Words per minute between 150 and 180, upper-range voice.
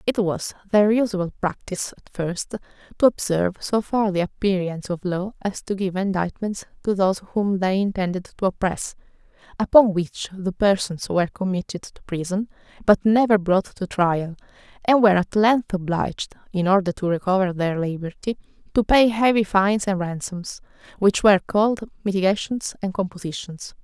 Yes: average, 155 wpm; high, 195 Hz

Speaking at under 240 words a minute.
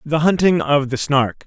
Yes: fast, 205 wpm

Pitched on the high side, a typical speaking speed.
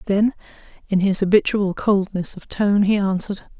Yes: high, 195 Hz; average, 150 wpm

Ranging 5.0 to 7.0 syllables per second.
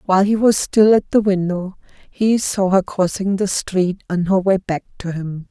No: 4.5 syllables/s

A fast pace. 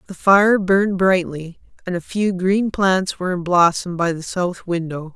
No: average, 185 wpm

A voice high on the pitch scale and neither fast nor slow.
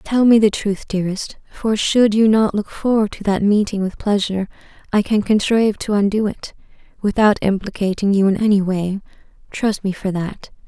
Yes: high, 205 Hz; average, 180 wpm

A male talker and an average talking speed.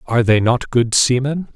Yes: male; average, 195 wpm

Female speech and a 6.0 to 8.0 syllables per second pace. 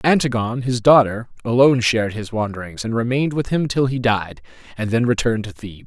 No: male; 6.3 syllables/s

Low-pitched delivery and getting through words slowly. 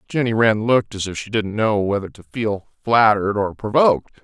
No: low, 105 Hz; average, 200 wpm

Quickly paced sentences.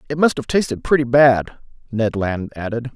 No: average, 185 wpm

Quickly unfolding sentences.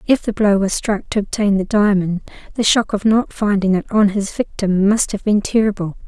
Yes: fast, 215 wpm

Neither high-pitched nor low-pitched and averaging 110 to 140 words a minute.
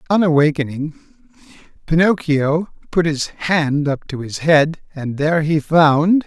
Yes: medium, 155 Hz; slow, 135 wpm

